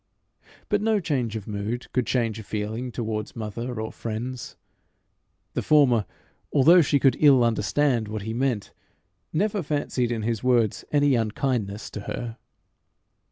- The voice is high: No, low, 120 Hz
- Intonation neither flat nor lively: Yes, average, 3.9 semitones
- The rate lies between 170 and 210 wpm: No, average, 145 wpm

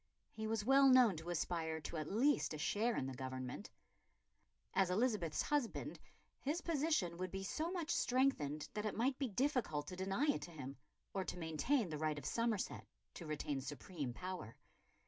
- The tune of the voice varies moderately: No, wide, 8.5 semitones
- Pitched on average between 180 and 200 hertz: Yes, high, 190 Hz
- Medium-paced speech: Yes, average, 180 wpm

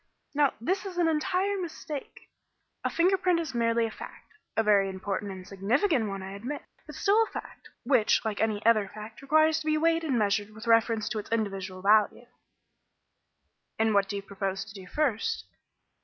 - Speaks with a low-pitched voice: No, high, 225 Hz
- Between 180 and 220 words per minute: Yes, average, 185 wpm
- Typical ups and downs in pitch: No, wide, 7.5 semitones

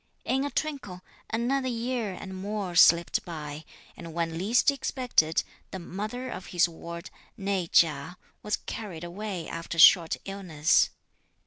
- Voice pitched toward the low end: No, medium, 185 Hz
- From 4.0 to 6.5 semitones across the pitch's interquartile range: Yes, average, 4.9 semitones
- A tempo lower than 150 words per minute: Yes, average, 140 wpm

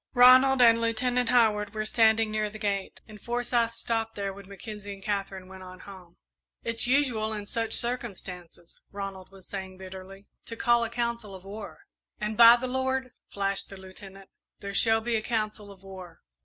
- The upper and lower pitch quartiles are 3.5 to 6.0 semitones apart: No, average, 3.1 semitones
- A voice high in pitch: Yes, high, 215 Hz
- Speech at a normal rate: Yes, average, 180 wpm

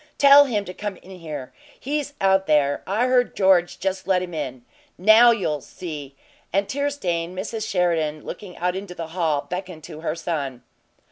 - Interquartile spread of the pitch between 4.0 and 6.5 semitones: Yes, average, 4.4 semitones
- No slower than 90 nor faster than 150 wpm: No, average, 180 wpm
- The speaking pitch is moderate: Yes, medium, 180 Hz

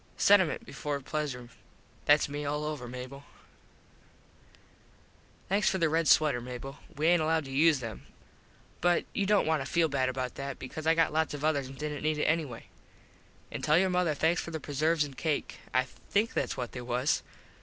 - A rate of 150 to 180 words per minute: No, average, 190 wpm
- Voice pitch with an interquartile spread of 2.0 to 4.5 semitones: Yes, average, 3.2 semitones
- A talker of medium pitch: Yes, medium, 150 Hz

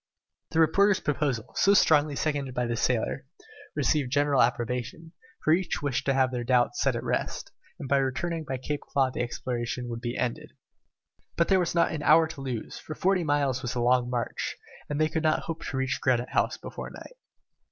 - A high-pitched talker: No, medium, 140 Hz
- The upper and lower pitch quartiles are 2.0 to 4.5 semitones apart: Yes, average, 4.1 semitones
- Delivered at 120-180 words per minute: No, average, 200 wpm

